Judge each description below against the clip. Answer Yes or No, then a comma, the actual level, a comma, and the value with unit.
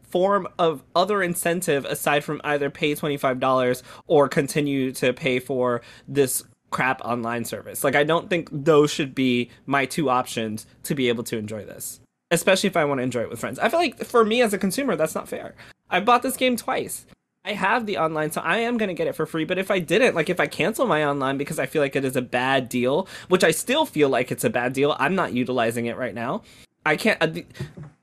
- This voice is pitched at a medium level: Yes, medium, 150 Hz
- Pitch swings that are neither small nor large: No, wide, 6.0 semitones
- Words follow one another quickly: Yes, fast, 235 wpm